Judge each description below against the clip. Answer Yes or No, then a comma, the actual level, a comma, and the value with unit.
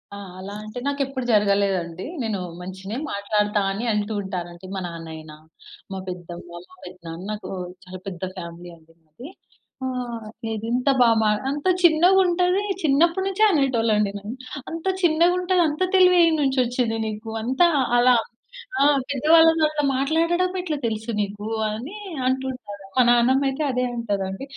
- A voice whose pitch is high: Yes, high, 230 Hz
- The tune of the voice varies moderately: No, wide, 7.7 semitones